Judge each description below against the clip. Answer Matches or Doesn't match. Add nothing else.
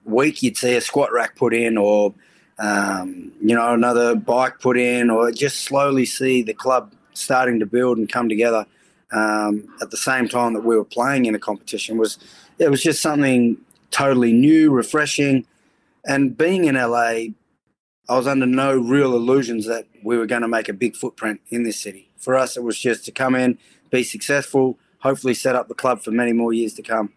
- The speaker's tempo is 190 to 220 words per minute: Matches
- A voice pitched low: Matches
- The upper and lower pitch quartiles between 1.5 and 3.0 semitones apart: Matches